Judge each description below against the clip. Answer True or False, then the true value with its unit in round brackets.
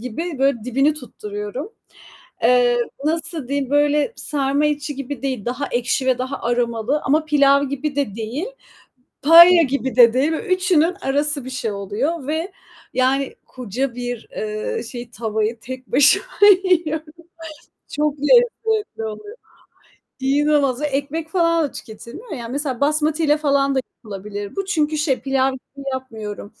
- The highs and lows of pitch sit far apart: False (3.8 semitones)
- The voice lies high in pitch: True (275 Hz)